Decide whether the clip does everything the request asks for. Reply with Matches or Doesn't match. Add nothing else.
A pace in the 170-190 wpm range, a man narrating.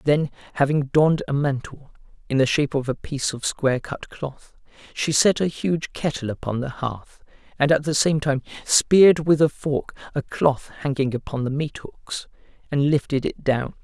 Matches